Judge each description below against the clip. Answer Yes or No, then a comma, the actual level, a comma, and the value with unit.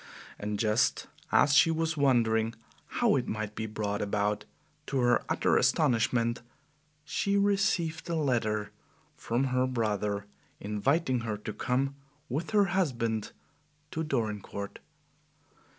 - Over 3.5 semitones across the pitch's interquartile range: Yes, average, 5.1 semitones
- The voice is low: Yes, low, 120 Hz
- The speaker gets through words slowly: Yes, slow, 120 wpm